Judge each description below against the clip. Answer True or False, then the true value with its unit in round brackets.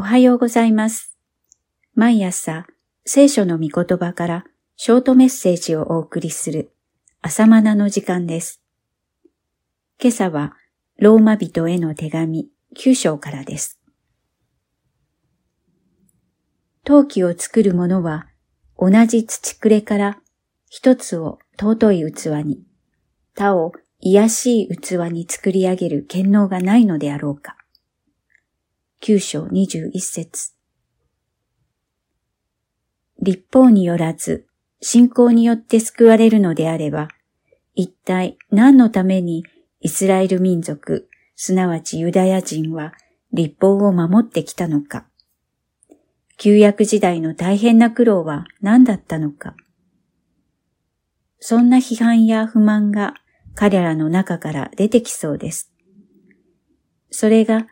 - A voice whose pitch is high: True (195 Hz)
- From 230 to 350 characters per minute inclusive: False (210 characters per minute)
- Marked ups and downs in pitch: False (5.0 semitones)